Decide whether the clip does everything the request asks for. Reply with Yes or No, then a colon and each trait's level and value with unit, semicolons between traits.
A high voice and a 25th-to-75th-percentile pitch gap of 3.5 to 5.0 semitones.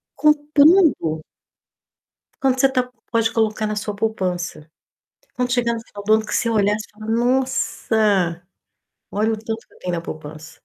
Yes: high, 220 Hz; average, 3.9 semitones